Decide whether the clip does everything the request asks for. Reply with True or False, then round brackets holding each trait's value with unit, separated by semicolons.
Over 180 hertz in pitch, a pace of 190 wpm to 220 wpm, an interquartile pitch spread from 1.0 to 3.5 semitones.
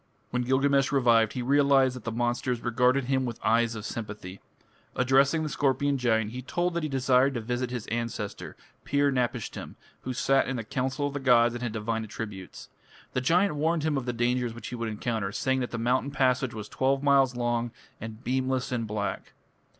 False (125 Hz; 195 wpm; 2.7 semitones)